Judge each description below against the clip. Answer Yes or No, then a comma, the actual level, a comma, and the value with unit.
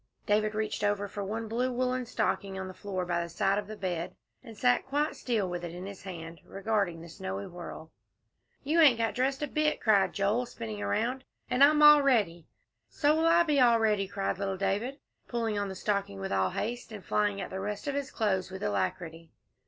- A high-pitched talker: Yes, high, 205 Hz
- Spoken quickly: Yes, fast, 215 wpm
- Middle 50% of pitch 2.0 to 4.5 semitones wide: No, average, 5.1 semitones